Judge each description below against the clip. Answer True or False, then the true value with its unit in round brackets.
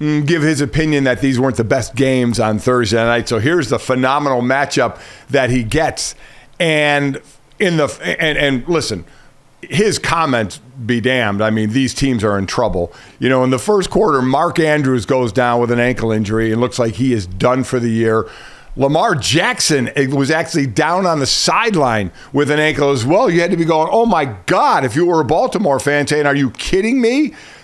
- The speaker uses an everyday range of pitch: True (4.0 semitones)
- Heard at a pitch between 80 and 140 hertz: True (135 Hz)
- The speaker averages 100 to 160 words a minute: False (200 wpm)